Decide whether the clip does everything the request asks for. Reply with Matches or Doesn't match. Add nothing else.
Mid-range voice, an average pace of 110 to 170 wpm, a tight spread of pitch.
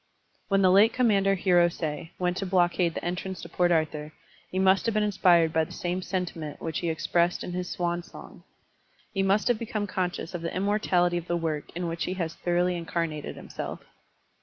Doesn't match